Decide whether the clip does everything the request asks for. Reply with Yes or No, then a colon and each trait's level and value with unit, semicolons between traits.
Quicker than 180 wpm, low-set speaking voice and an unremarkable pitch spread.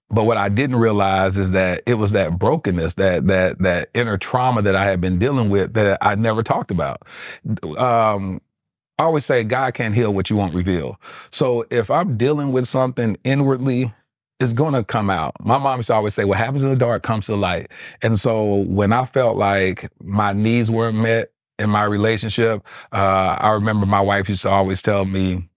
Yes: fast, 205 wpm; low, 105 Hz; average, 3.6 semitones